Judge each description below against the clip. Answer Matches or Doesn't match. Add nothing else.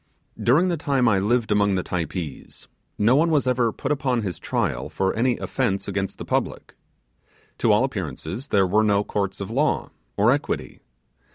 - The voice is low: Matches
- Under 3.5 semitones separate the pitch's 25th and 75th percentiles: Doesn't match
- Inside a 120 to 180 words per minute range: Matches